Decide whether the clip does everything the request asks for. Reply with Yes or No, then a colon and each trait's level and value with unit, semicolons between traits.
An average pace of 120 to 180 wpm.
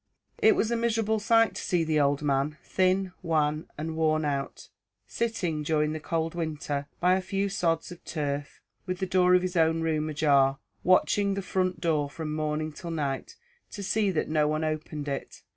No: average, 190 wpm